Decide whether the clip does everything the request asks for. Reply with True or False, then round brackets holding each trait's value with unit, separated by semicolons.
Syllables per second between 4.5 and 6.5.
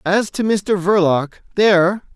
False (4.1 syllables/s)